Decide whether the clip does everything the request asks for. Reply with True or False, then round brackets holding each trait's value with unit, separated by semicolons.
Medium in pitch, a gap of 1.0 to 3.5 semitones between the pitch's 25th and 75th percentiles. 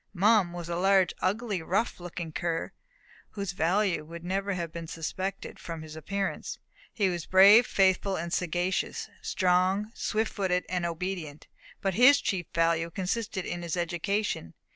True (180 Hz; 2.6 semitones)